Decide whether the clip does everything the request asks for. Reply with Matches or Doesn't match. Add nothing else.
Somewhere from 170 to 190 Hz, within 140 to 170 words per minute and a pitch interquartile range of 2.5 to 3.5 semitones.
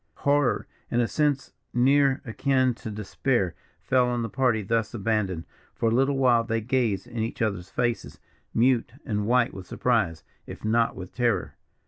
Doesn't match